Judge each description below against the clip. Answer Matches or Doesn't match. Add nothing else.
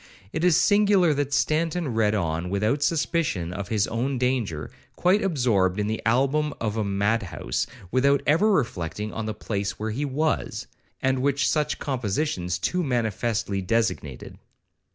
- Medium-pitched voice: Doesn't match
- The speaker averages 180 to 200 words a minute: Doesn't match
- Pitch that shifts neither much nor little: Doesn't match